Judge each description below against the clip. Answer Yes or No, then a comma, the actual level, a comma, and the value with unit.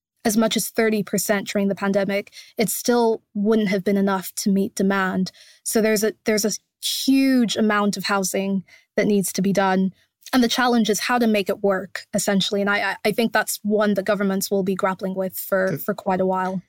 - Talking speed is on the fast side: Yes, fast, 210 wpm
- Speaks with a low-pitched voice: No, high, 205 Hz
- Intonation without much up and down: Yes, narrow, 2.0 semitones